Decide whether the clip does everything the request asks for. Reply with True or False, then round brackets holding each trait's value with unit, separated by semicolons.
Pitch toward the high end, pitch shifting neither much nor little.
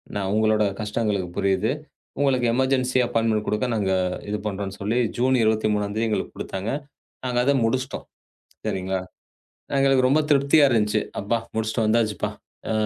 False (110 Hz; 3.4 semitones)